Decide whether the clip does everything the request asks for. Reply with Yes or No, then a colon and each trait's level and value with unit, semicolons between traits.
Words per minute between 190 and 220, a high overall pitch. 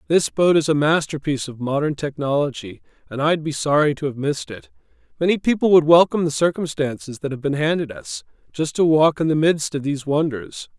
No: average, 200 wpm; medium, 150 Hz